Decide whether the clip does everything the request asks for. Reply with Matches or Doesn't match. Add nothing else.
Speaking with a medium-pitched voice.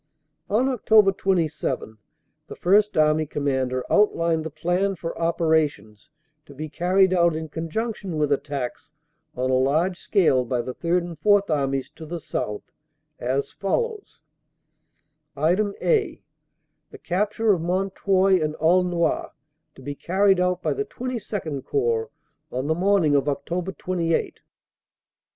Matches